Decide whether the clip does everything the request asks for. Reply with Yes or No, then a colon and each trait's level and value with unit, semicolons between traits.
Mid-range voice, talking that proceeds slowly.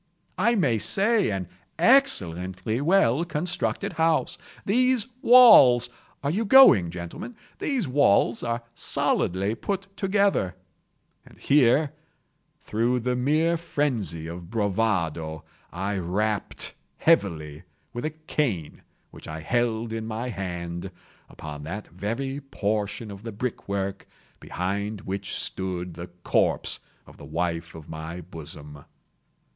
No: low, 110 Hz; slow, 115 wpm